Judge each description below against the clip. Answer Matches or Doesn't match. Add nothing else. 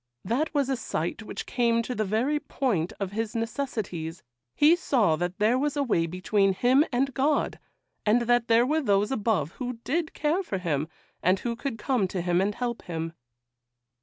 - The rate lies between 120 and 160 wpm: Doesn't match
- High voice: Matches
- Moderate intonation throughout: Doesn't match